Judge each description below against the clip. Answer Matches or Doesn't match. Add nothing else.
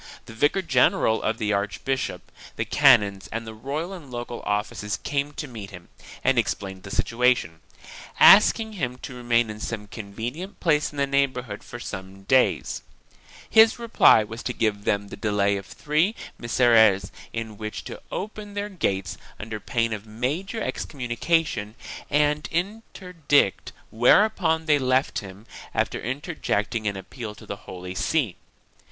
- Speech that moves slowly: Doesn't match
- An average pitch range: Doesn't match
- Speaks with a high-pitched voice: Doesn't match